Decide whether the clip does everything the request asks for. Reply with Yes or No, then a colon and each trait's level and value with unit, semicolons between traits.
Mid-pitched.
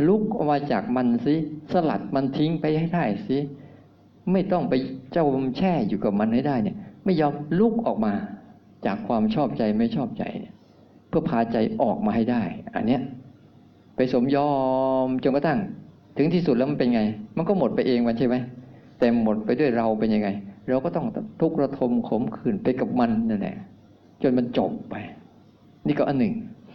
Yes: medium, 150 Hz